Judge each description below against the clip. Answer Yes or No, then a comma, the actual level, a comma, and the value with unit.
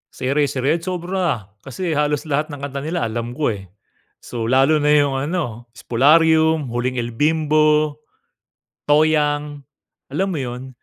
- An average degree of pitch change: Yes, average, 3.4 semitones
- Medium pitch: Yes, medium, 145 Hz